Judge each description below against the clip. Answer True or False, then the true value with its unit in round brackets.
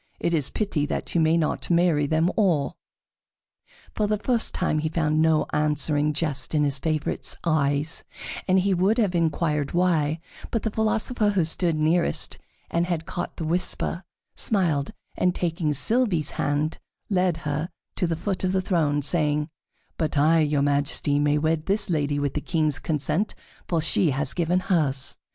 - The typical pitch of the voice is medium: True (160 Hz)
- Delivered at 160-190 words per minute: True (165 wpm)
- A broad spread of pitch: False (3.2 semitones)